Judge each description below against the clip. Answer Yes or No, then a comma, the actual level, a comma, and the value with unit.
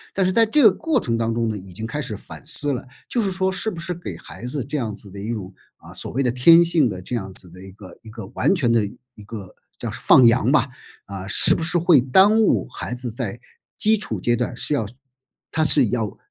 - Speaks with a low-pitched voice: Yes, low, 125 Hz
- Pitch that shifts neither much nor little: No, wide, 7.5 semitones